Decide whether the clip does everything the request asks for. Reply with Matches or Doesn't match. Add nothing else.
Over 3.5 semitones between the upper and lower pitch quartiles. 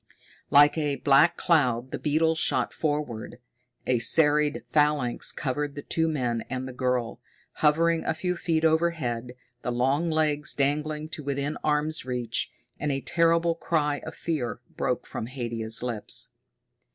Matches